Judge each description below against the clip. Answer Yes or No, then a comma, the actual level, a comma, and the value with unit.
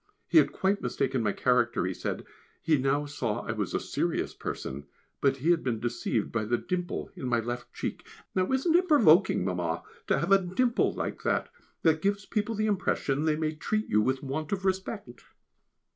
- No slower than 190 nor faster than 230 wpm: Yes, average, 195 wpm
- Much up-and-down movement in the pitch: Yes, wide, 8.1 semitones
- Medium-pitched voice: Yes, medium, 150 Hz